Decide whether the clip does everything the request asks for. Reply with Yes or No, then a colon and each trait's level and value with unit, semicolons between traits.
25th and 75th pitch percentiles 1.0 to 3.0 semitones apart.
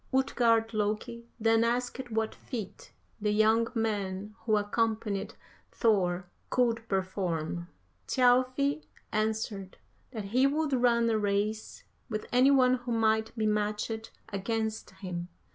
Yes: narrow, 2.4 semitones